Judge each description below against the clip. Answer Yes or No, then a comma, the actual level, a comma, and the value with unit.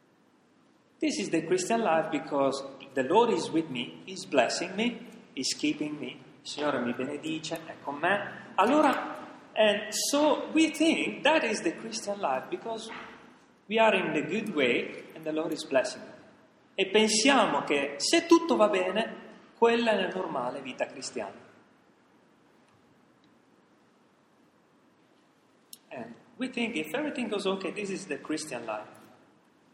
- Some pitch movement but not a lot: No, wide, 8.8 semitones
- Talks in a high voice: Yes, high, 215 Hz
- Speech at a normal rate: Yes, average, 145 wpm